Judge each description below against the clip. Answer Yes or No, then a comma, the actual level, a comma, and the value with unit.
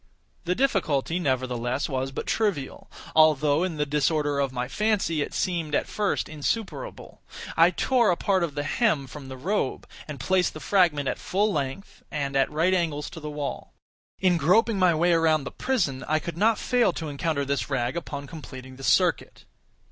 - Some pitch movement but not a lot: Yes, average, 4.8 semitones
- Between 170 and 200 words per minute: Yes, average, 185 wpm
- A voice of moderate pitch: Yes, medium, 155 Hz